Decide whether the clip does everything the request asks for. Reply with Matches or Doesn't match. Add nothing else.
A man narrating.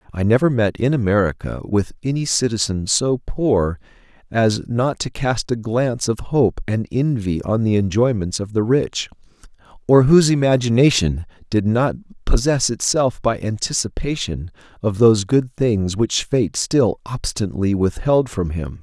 Matches